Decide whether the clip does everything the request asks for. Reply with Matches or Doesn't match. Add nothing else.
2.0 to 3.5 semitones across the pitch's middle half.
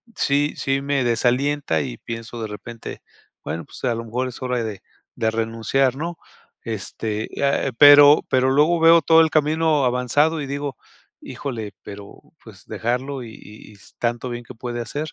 Doesn't match